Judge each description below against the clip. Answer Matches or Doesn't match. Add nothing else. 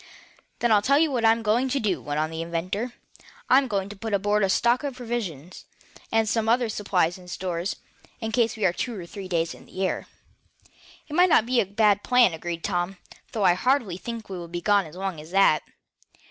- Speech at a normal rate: Doesn't match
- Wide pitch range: Doesn't match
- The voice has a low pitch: Doesn't match